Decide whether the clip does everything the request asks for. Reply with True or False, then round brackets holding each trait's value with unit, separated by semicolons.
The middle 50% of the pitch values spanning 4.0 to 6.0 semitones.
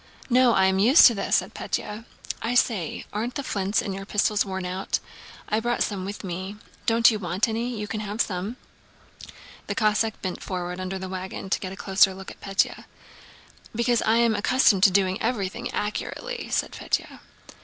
False (3.3 semitones)